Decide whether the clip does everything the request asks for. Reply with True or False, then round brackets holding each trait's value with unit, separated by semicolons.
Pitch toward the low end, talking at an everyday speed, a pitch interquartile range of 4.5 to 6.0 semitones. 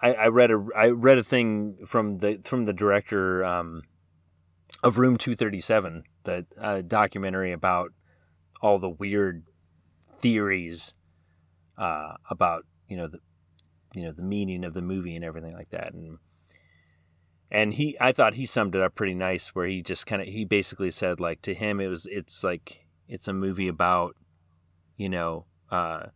False (95 Hz; 170 wpm; 3.6 semitones)